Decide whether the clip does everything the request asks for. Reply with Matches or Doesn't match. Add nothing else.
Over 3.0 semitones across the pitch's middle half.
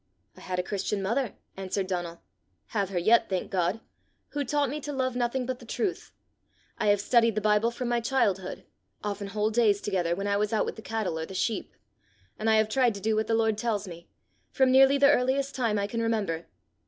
Matches